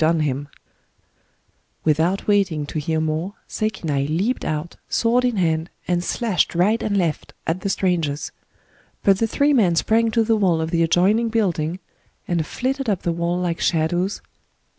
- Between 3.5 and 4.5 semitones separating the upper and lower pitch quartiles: No, average, 5.0 semitones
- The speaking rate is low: No, average, 160 wpm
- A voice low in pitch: No, medium, 175 Hz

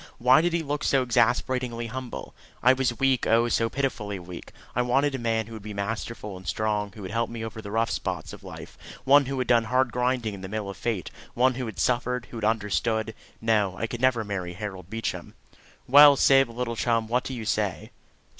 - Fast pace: Yes, fast, 220 wpm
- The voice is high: No, low, 115 Hz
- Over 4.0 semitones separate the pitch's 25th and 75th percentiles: No, average, 3.0 semitones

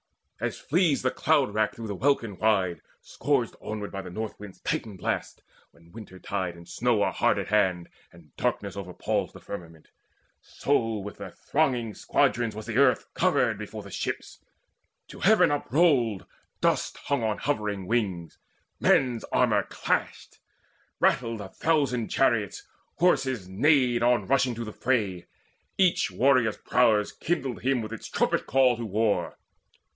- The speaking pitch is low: Yes, low, 115 Hz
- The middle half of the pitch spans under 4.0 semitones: No, average, 4.5 semitones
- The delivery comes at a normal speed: Yes, average, 150 wpm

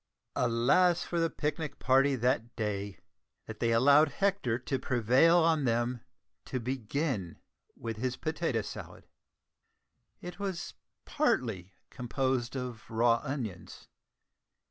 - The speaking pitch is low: Yes, low, 125 Hz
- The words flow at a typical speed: No, slow, 115 wpm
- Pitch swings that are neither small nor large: Yes, average, 4.5 semitones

